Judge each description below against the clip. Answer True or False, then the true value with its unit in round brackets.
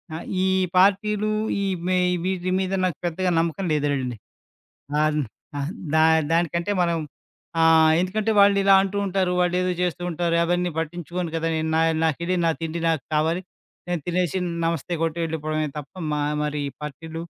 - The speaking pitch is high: False (170 Hz)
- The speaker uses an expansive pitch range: False (2.4 semitones)